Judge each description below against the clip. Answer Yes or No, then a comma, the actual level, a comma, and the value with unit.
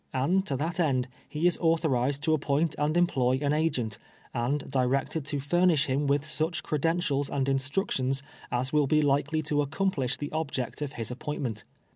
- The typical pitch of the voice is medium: Yes, medium, 145 Hz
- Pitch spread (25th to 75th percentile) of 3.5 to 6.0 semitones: No, average, 2.9 semitones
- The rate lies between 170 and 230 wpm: Yes, average, 175 wpm